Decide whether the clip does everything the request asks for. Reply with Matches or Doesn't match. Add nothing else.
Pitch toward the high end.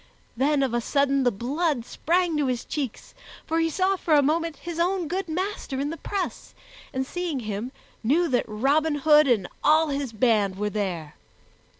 Matches